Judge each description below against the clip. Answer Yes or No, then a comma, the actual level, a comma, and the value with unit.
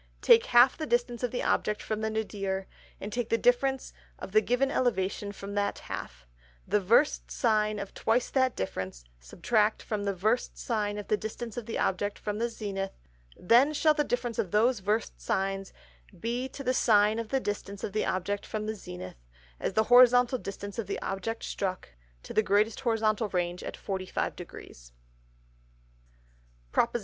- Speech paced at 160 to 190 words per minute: Yes, average, 180 wpm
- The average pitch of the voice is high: Yes, high, 215 Hz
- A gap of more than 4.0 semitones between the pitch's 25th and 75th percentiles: No, average, 3.4 semitones